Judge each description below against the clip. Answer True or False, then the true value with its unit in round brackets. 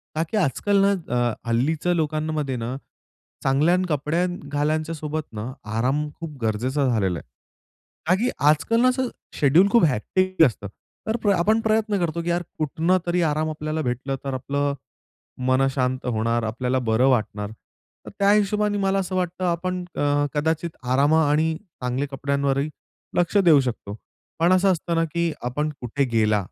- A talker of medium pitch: True (150 Hz)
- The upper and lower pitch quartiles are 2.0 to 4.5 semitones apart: False (5.2 semitones)